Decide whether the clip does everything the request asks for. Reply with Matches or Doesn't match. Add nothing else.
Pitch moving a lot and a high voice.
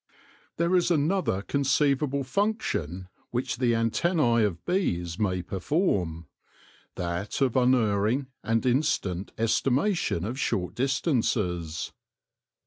Doesn't match